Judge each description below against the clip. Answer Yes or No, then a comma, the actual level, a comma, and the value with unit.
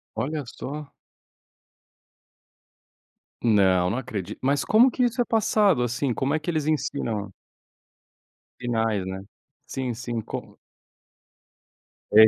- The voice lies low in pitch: Yes, low, 125 Hz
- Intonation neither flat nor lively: No, wide, 5.7 semitones